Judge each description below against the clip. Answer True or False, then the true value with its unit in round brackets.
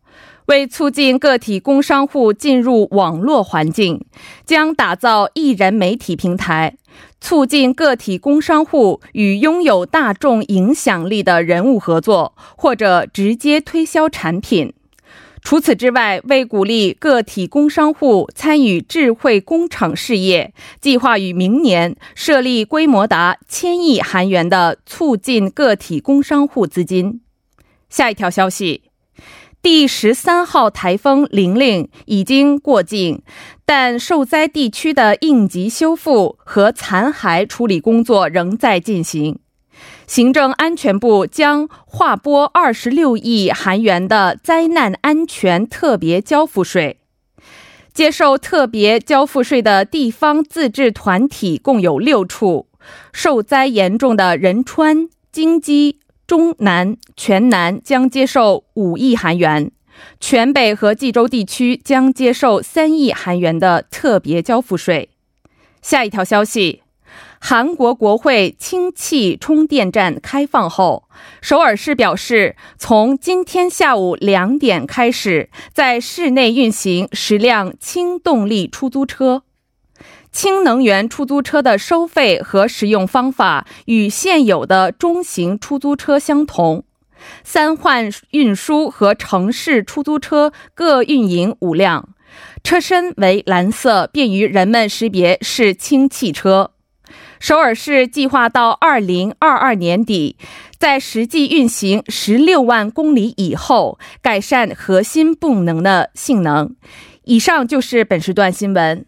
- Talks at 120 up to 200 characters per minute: True (195 characters per minute)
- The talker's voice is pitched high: True (245 Hz)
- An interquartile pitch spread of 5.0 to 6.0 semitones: False (6.6 semitones)